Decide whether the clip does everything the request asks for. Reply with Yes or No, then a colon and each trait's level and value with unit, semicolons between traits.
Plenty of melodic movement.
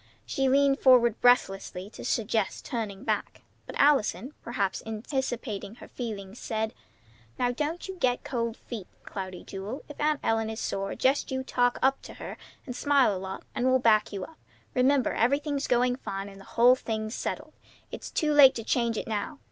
No: average, 3.7 semitones